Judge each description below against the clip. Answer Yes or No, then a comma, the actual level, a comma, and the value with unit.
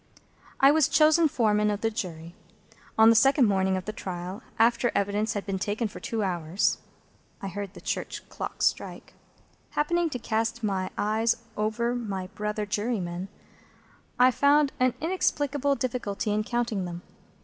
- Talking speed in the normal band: Yes, average, 155 wpm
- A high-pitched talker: Yes, high, 215 Hz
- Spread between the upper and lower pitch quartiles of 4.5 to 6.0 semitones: No, average, 4.0 semitones